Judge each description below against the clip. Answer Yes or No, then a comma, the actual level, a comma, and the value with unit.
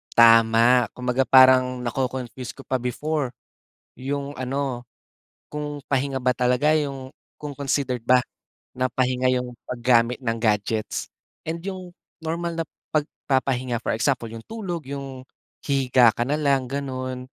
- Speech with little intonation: Yes, narrow, 2.3 semitones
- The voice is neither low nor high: No, low, 130 Hz